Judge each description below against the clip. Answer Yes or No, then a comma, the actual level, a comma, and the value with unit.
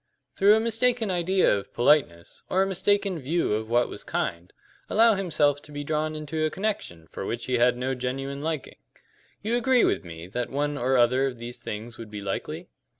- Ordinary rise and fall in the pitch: No, wide, 7.8 semitones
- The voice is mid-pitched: Yes, medium, 145 Hz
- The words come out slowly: No, average, 200 wpm